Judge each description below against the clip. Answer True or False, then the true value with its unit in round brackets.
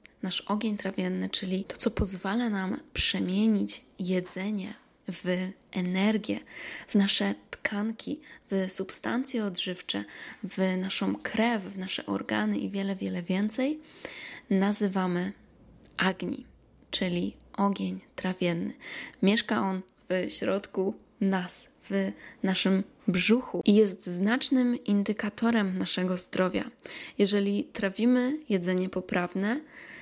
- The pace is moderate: False (100 wpm)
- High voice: True (195 Hz)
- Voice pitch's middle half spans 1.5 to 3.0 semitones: True (2.7 semitones)